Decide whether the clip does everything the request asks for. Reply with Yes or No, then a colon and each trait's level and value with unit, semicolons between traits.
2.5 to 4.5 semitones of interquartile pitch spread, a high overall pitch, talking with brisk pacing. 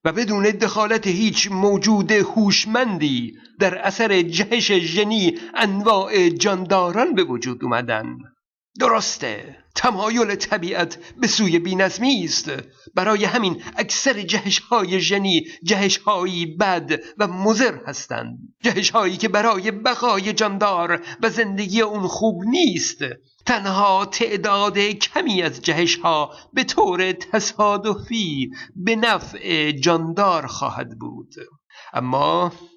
No: average, 3.6 semitones; high, 200 Hz; slow, 105 wpm